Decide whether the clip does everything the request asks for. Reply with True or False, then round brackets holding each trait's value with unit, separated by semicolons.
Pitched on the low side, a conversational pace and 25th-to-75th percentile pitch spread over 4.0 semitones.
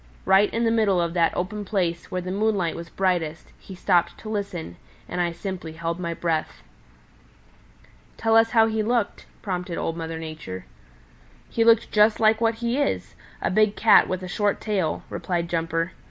False (185 Hz; 180 wpm; 4.4 semitones)